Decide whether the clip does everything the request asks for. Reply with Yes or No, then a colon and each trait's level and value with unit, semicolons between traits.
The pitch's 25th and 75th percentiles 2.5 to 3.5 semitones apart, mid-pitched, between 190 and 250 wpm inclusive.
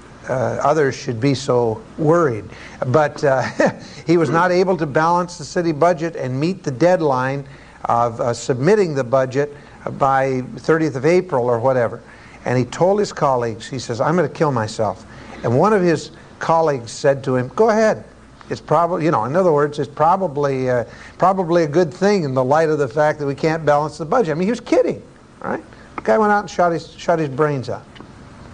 No: average, 4.7 semitones; medium, 150 Hz; fast, 205 wpm